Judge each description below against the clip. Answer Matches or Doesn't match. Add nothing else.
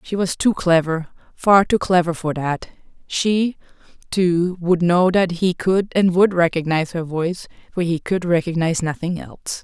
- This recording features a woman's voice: Matches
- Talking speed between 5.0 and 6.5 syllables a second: Doesn't match